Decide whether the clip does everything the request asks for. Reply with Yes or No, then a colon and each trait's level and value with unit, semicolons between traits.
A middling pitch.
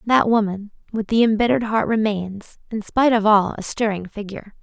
No: high, 215 Hz